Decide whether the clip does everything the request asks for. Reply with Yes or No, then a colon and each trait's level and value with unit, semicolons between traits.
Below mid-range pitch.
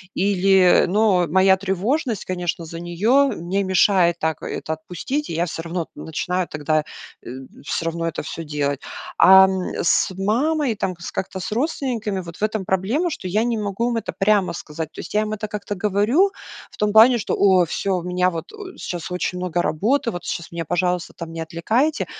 No: high, 190 Hz